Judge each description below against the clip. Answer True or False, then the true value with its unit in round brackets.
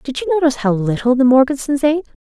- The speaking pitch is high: True (270 Hz)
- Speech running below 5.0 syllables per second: False (6.9 syllables/s)